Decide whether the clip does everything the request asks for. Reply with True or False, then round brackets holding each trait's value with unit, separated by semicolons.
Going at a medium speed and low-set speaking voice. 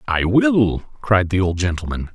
True (170 wpm; 105 Hz)